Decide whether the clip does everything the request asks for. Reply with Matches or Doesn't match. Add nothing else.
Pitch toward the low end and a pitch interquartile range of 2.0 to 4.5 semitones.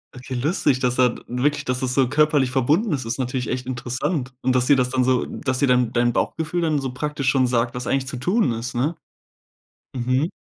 Matches